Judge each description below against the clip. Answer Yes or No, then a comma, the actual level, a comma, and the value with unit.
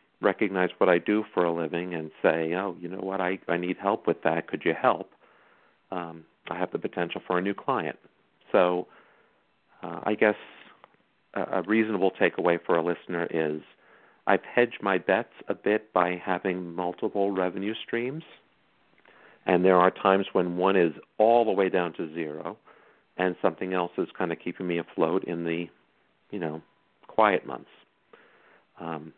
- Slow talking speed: No, average, 170 wpm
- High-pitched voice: No, very low, 90 Hz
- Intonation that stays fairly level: Yes, narrow, 2.2 semitones